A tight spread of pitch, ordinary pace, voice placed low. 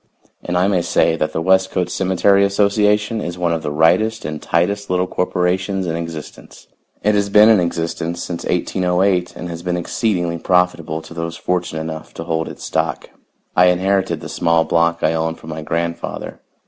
Yes: narrow, 2.3 semitones; average, 180 wpm; very low, 90 Hz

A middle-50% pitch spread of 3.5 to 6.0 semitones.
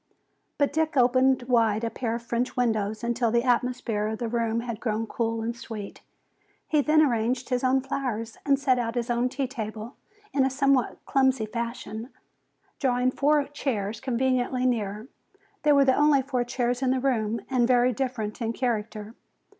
No: narrow, 2.6 semitones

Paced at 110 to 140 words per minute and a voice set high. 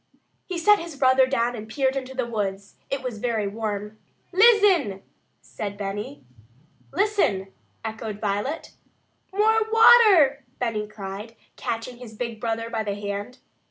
Yes: slow, 135 wpm; high, 230 Hz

